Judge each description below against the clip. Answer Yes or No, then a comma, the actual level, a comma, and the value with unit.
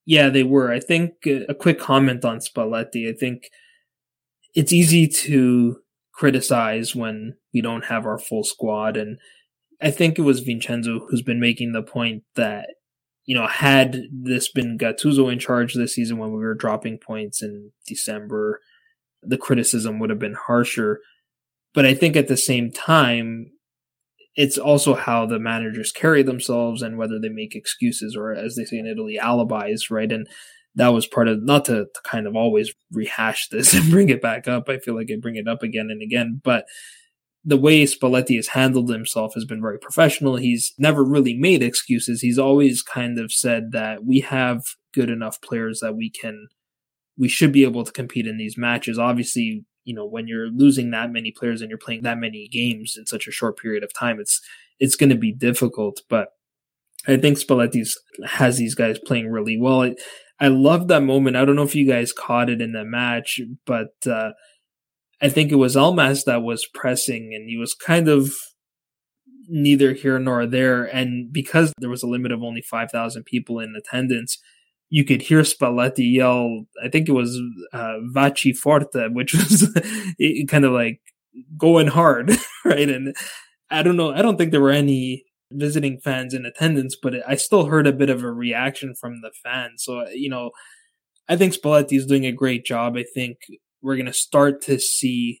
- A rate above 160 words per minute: Yes, average, 190 wpm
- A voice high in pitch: No, low, 125 Hz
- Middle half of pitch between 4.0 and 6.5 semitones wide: No, average, 3.5 semitones